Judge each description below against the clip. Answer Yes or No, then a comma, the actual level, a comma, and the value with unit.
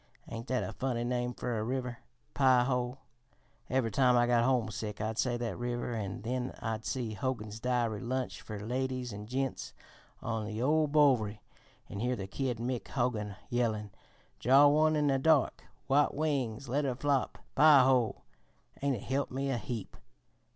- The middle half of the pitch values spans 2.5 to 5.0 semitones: Yes, average, 2.9 semitones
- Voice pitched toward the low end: Yes, low, 125 Hz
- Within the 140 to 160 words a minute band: No, average, 170 wpm